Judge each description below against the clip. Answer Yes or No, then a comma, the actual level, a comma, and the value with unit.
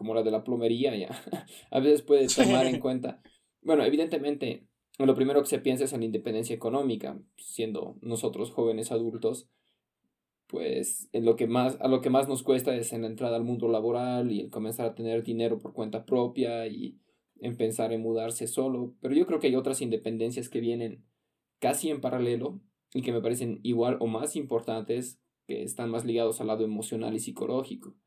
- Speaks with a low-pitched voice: Yes, low, 120 Hz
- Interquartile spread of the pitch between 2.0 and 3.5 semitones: Yes, narrow, 2.5 semitones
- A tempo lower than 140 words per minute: No, fast, 190 wpm